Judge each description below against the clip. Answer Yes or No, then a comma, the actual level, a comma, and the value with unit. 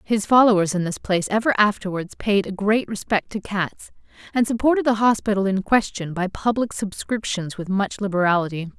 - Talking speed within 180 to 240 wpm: No, average, 170 wpm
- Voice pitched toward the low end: No, high, 205 Hz